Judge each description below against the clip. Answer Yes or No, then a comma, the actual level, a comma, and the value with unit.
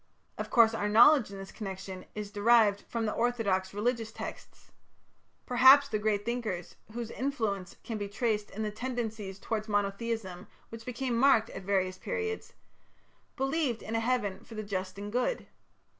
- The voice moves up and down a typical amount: Yes, average, 3.1 semitones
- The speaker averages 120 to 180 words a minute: Yes, average, 160 wpm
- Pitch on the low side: No, high, 220 Hz